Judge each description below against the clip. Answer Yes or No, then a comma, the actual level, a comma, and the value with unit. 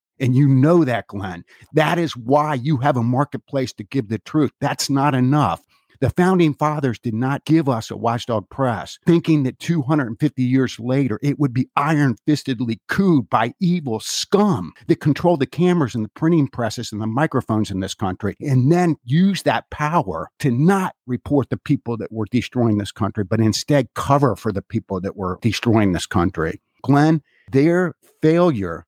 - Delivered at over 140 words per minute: Yes, average, 175 wpm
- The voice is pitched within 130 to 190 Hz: Yes, low, 135 Hz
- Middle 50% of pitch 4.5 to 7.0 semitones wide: Yes, average, 5.0 semitones